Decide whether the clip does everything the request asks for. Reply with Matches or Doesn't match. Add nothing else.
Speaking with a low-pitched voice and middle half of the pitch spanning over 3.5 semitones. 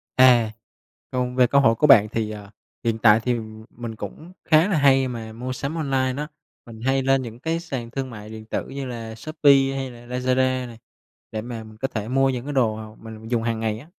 Doesn't match